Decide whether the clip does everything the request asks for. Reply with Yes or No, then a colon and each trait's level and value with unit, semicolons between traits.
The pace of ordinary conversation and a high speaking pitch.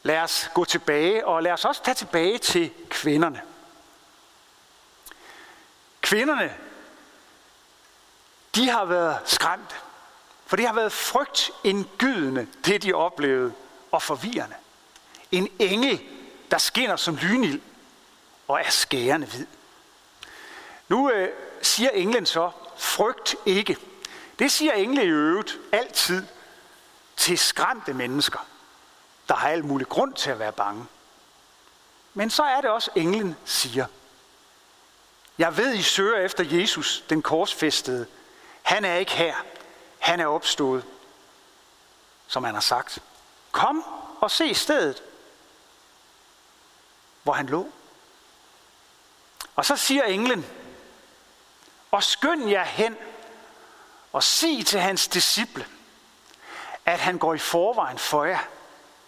No: slow, 120 wpm; high, 225 Hz